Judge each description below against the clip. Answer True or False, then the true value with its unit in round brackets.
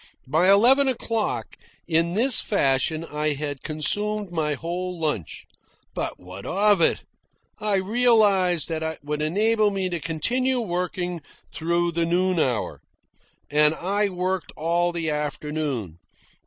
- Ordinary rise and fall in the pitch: True (4.7 semitones)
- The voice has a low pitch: False (175 Hz)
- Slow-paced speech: True (130 wpm)